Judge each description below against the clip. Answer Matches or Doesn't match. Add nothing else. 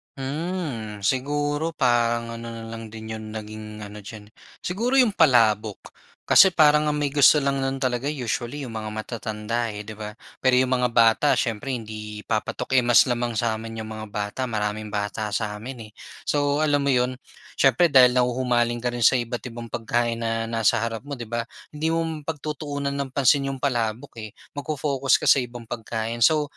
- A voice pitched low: Matches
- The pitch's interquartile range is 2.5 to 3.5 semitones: Doesn't match